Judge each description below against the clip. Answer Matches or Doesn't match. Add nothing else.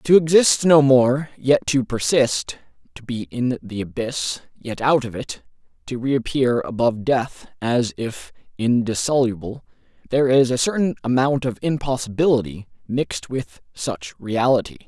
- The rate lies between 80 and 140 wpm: Matches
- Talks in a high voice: Doesn't match